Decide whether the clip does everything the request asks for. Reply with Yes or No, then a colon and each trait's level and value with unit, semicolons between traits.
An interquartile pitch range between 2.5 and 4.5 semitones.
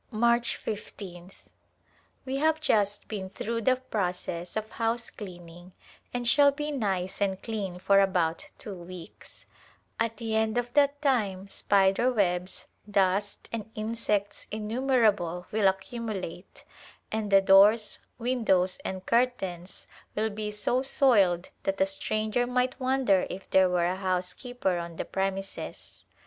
Yes: average, 4.0 semitones